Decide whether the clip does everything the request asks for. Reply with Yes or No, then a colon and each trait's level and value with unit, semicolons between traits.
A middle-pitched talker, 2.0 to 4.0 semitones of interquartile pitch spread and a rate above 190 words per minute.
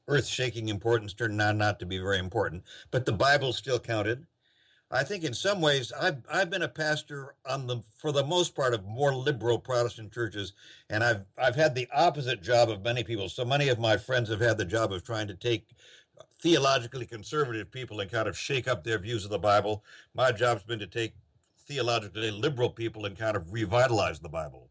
No: low, 120 Hz; average, 3.7 semitones; fast, 205 wpm